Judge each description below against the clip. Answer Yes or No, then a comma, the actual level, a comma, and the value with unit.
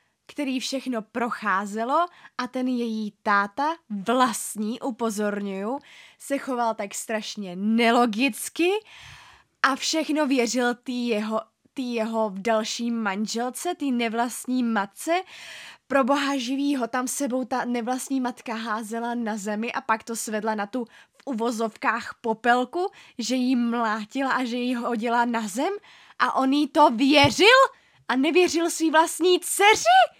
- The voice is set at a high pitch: Yes, high, 245 Hz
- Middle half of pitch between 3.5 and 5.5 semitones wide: Yes, average, 3.8 semitones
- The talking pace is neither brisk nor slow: Yes, average, 135 wpm